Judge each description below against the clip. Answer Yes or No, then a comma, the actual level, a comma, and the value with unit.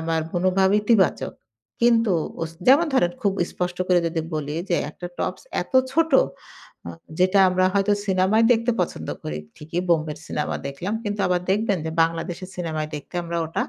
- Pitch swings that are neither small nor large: Yes, average, 3.9 semitones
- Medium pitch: Yes, medium, 180 Hz